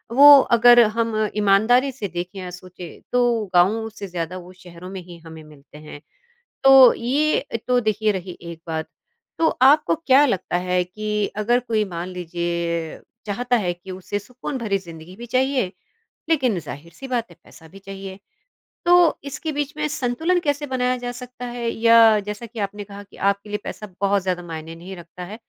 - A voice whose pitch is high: Yes, high, 210 Hz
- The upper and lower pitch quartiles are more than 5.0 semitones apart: Yes, wide, 5.6 semitones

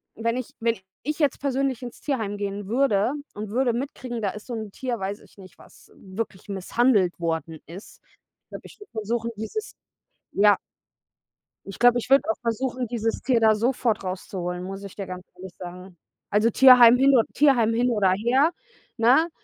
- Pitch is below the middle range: No, high, 225 Hz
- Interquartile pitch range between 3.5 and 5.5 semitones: Yes, average, 4.1 semitones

